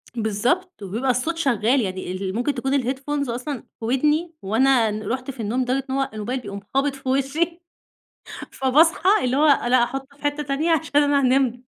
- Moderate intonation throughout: Yes, average, 3.3 semitones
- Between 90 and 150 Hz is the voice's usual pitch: No, very high, 265 Hz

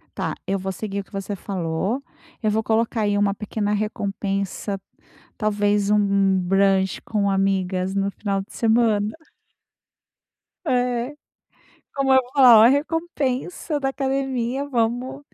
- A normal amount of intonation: Yes, average, 4.0 semitones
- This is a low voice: No, high, 210 Hz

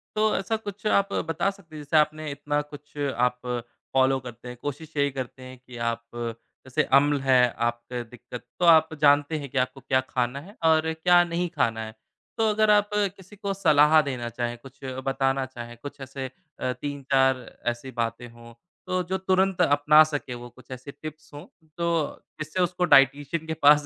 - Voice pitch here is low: No, medium, 145 Hz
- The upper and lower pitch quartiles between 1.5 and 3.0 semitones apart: No, average, 4.2 semitones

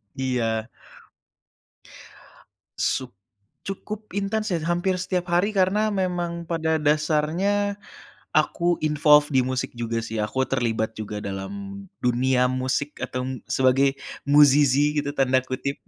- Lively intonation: Yes, wide, 5.7 semitones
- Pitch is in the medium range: Yes, medium, 150 Hz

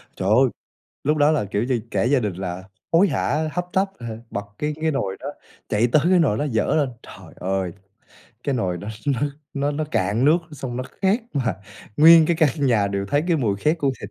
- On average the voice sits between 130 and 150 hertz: Yes, low, 135 Hz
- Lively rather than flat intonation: Yes, wide, 7.0 semitones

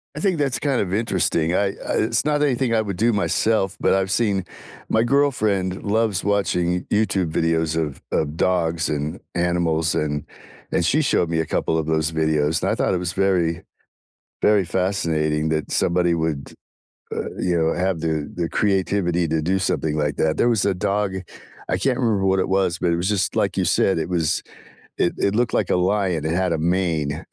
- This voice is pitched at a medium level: No, very low, 90 Hz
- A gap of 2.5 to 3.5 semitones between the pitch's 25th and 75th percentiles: No, average, 3.9 semitones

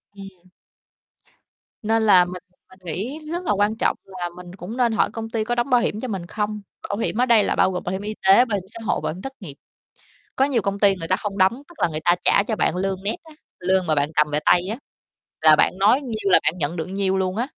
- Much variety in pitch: No, average, 3.8 semitones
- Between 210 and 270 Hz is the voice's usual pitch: No, high, 200 Hz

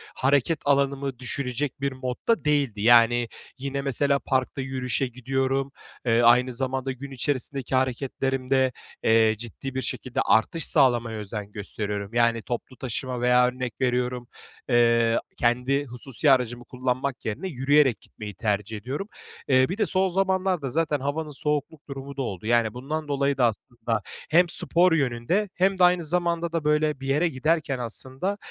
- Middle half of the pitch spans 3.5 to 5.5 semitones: No, average, 3.1 semitones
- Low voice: Yes, low, 130 Hz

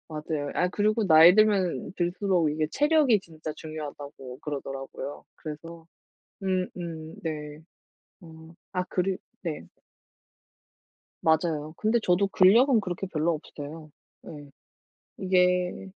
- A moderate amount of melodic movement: Yes, average, 3.5 semitones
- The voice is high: No, medium, 165 Hz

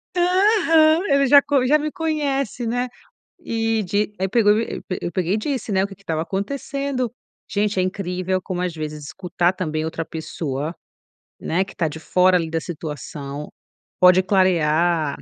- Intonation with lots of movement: Yes, wide, 7.3 semitones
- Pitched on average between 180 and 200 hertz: Yes, high, 190 Hz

